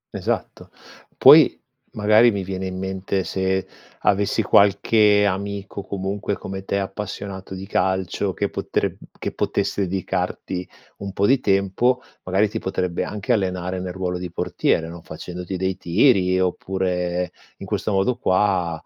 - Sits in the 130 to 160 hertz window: No, very low, 95 Hz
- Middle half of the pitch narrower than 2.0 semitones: Yes, narrow, 1.6 semitones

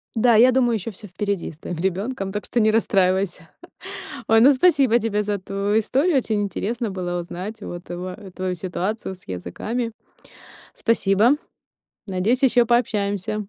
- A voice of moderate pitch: No, high, 205 Hz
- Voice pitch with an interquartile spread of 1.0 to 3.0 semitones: No, average, 3.7 semitones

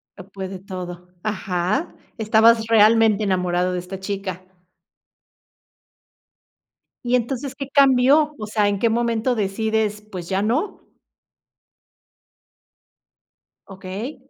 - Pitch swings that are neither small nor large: Yes, average, 3.6 semitones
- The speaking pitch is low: No, high, 215 Hz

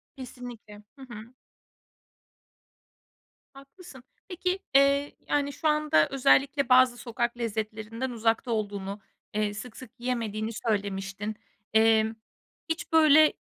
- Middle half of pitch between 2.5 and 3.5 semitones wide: No, average, 4.4 semitones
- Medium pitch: No, high, 240 Hz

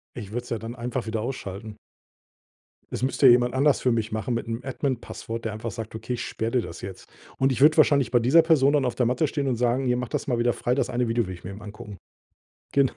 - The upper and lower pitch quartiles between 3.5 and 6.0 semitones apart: No, average, 2.7 semitones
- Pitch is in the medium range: No, low, 120 Hz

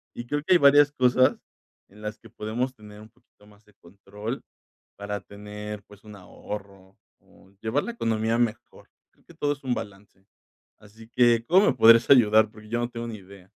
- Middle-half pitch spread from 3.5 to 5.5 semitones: No, average, 2.9 semitones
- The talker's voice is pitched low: Yes, low, 110 Hz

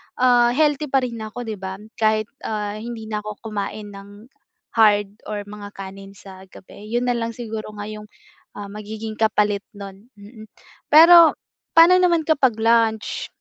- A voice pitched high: Yes, high, 215 Hz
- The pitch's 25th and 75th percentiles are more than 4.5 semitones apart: No, average, 2.7 semitones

